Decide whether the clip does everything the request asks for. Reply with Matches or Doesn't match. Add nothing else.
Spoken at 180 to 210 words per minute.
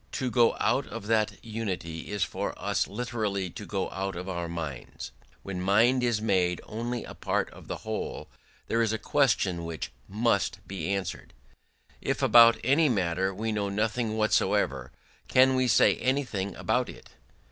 Doesn't match